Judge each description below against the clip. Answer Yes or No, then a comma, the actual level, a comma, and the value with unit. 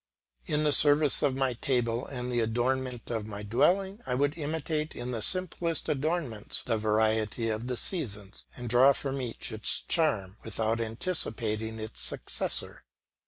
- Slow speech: No, average, 155 wpm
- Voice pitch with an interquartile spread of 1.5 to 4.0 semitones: No, average, 4.8 semitones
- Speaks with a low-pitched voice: Yes, low, 125 Hz